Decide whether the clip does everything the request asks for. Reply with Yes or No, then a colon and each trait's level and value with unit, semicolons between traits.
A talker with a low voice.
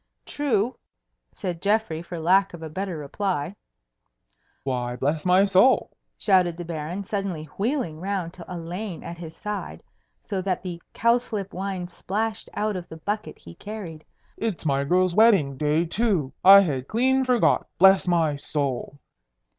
No: medium, 185 Hz